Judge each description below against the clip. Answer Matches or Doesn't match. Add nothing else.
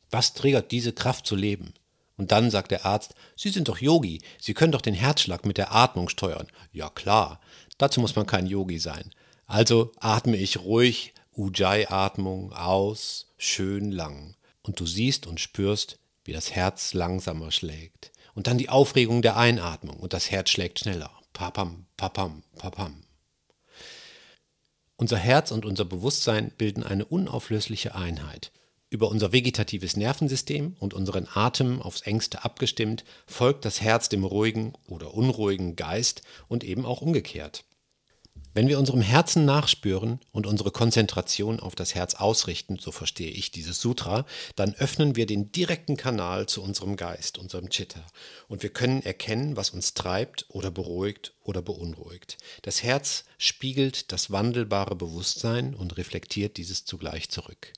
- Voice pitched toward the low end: Matches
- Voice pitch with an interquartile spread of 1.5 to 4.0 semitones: Doesn't match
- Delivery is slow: Doesn't match